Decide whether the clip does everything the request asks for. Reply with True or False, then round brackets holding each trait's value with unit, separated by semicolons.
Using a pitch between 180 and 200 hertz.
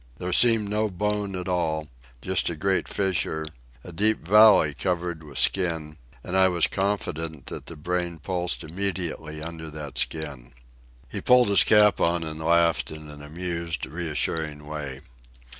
False (85 Hz)